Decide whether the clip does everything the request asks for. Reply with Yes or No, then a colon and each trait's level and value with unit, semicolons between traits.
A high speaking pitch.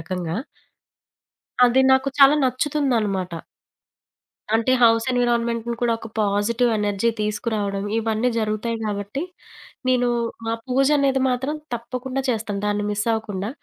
Yes: high, 230 Hz